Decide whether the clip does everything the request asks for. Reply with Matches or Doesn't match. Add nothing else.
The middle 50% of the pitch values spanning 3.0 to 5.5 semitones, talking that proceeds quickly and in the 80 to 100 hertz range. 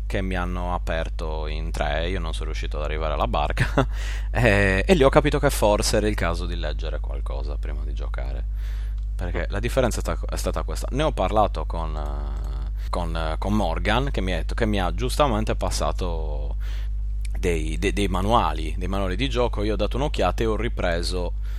Matches